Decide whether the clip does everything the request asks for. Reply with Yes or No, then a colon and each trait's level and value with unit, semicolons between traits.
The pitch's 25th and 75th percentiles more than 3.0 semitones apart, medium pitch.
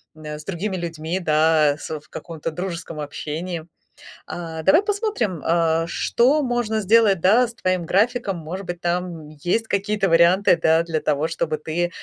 Yes: average, 3.8 semitones; medium, 175 Hz